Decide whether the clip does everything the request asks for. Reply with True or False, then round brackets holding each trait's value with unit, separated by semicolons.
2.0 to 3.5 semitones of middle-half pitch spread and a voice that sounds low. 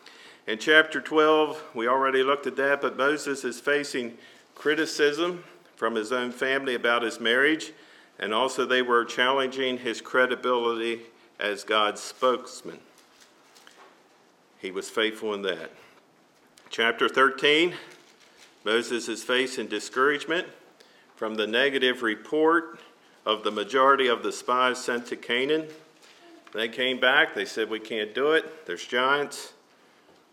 False (3.9 semitones; 125 Hz)